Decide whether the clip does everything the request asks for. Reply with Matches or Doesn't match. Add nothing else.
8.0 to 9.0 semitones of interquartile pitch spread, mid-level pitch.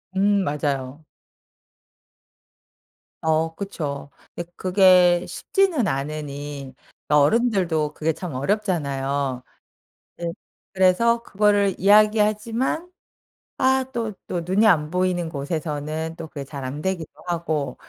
Doesn't match